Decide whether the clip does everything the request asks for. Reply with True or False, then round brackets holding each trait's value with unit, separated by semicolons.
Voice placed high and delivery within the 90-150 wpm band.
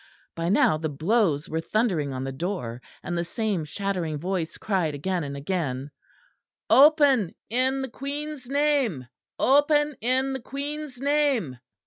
True (200 Hz; 140 wpm)